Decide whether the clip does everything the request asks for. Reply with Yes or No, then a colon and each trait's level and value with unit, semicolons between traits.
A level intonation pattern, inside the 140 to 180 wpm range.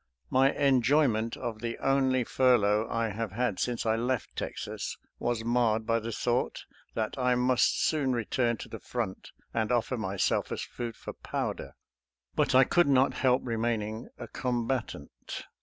Yes: narrow, 2.3 semitones; average, 160 wpm